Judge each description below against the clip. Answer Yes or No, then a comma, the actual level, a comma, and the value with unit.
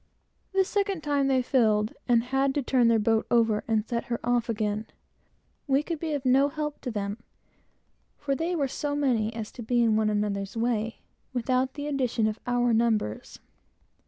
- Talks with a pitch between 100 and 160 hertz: No, high, 245 Hz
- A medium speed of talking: Yes, average, 185 wpm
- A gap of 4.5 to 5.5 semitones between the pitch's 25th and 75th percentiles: No, average, 4.0 semitones